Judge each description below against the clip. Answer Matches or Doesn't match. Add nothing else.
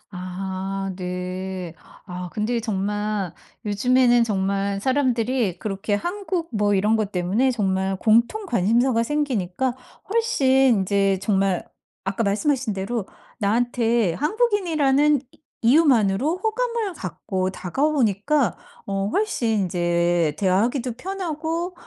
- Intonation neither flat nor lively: Doesn't match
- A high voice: Matches